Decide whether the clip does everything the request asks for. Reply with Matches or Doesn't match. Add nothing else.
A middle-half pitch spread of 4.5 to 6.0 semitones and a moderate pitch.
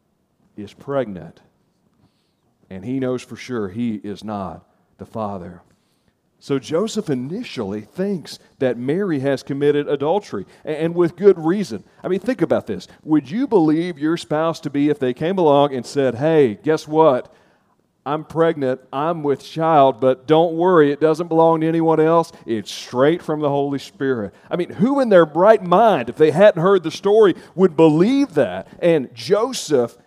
Matches